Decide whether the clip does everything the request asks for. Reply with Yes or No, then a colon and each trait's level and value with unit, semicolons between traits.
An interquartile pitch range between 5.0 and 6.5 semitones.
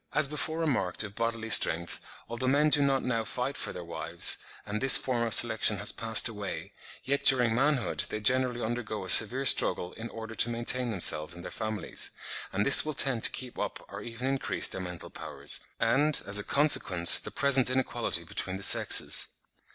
No: average, 4.3 semitones